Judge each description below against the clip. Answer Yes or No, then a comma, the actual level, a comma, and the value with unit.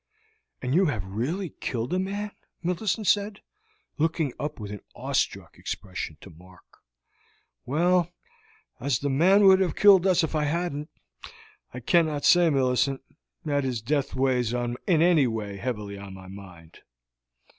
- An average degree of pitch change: No, wide, 7.7 semitones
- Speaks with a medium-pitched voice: Yes, medium, 145 Hz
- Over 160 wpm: No, average, 145 wpm